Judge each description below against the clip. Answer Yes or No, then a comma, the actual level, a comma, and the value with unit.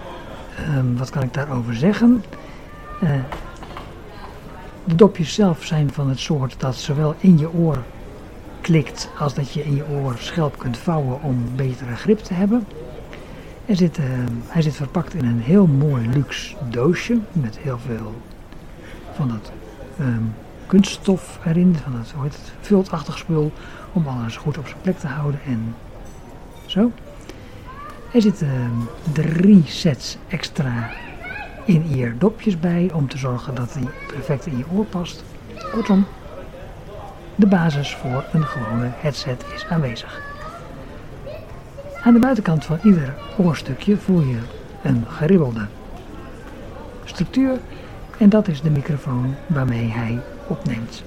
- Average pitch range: No, wide, 6.0 semitones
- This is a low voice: No, medium, 145 Hz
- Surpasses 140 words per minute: No, slow, 135 wpm